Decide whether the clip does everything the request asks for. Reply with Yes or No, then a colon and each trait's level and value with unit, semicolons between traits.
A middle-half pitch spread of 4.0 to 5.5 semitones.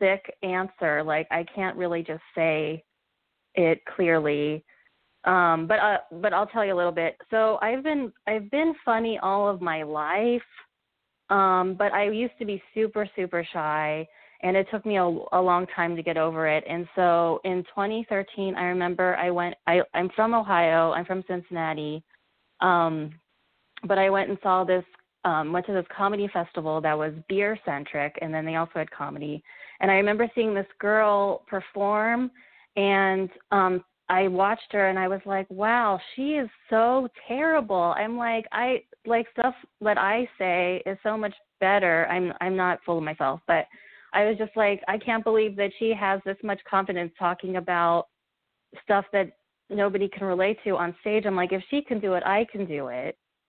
No: average, 3.5 semitones